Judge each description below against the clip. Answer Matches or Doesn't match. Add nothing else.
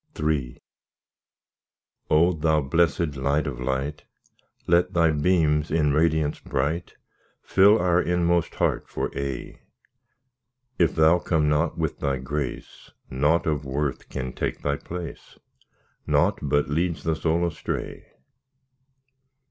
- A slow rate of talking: Matches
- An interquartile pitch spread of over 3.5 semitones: Doesn't match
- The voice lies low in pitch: Matches